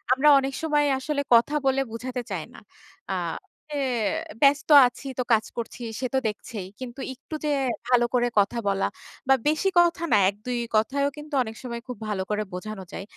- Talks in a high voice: Yes, very high, 250 Hz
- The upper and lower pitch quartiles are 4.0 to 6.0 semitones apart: Yes, average, 4.3 semitones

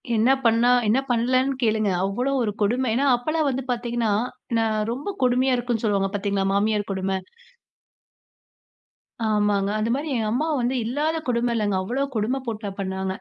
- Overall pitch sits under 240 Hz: Yes, high, 230 Hz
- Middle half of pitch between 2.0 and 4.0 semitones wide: Yes, average, 3.4 semitones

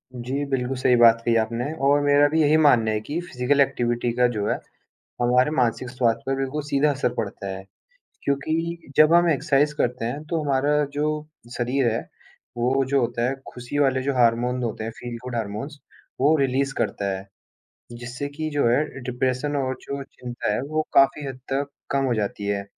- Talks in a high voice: No, low, 130 Hz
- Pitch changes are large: No, average, 3.1 semitones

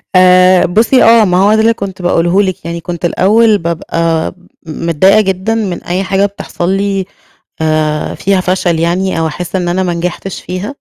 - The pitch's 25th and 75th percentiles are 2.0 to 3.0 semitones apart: Yes, average, 2.7 semitones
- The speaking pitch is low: No, medium, 185 Hz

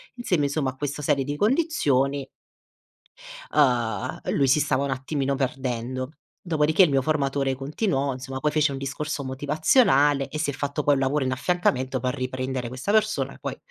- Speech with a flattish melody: Yes, narrow, 2.3 semitones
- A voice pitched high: No, medium, 140 Hz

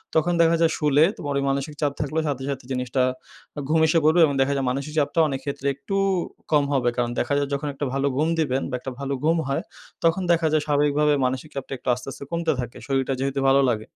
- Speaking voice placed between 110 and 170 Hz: Yes, medium, 140 Hz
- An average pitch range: No, narrow, 2.3 semitones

